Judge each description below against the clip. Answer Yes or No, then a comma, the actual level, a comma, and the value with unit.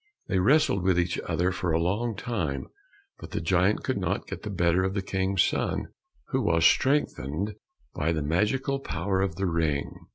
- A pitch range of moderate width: Yes, average, 3.4 semitones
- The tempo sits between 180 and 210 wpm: Yes, average, 185 wpm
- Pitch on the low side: Yes, very low, 95 Hz